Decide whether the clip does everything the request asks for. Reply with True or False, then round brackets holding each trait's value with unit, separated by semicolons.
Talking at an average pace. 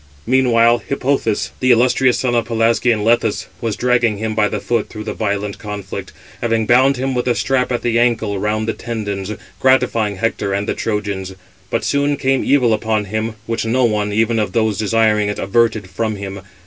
True (185 wpm)